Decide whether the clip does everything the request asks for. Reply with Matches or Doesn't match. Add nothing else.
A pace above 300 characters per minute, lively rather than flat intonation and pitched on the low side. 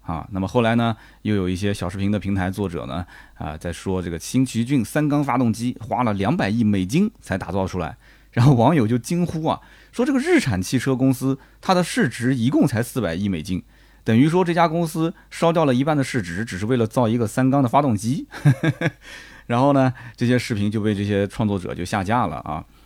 Matches